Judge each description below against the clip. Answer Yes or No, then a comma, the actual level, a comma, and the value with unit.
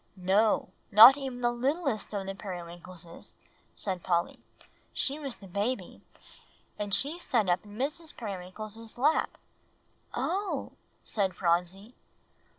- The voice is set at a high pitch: Yes, high, 210 Hz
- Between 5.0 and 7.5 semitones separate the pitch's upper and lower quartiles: Yes, wide, 5.6 semitones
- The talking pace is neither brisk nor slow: No, slow, 120 wpm